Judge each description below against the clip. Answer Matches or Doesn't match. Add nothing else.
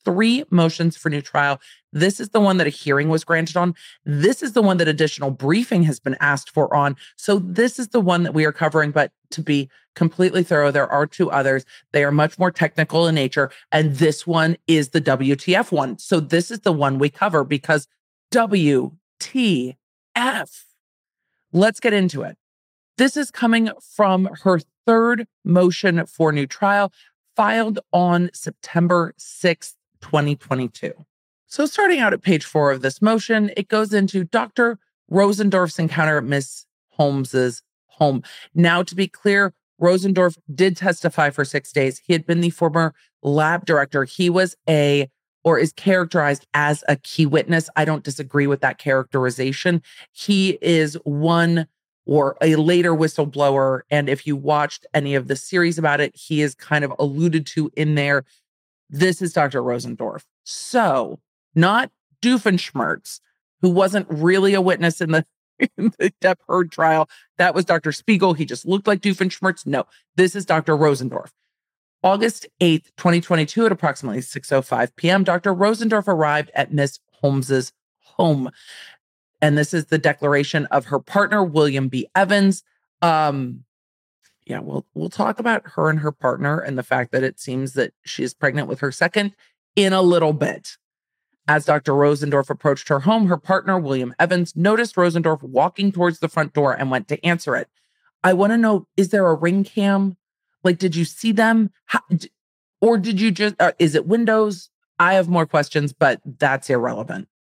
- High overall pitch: Doesn't match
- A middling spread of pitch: Matches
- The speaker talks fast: Doesn't match